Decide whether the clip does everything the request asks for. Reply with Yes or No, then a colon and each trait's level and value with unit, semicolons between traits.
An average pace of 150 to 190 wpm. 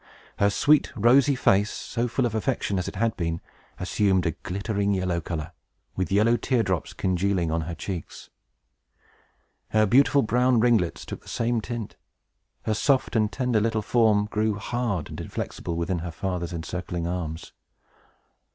Yes: average, 155 wpm